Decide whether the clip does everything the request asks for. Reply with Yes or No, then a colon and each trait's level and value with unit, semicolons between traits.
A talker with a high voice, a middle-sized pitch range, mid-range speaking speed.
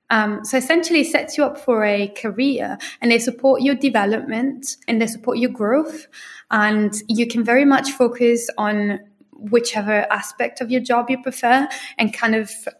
Yes: high, 240 Hz; average, 3.4 semitones; average, 175 wpm